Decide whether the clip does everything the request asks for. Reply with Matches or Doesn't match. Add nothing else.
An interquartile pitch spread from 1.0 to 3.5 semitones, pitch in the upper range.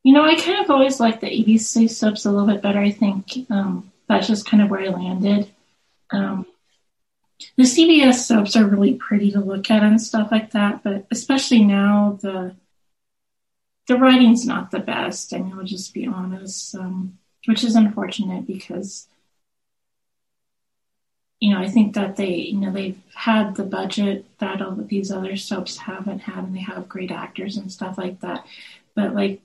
Matches